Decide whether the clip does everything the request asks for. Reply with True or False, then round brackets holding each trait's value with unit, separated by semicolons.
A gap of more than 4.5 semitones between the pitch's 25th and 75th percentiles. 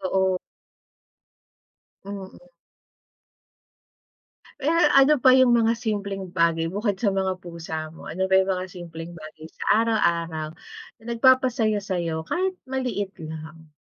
True (5.1 semitones)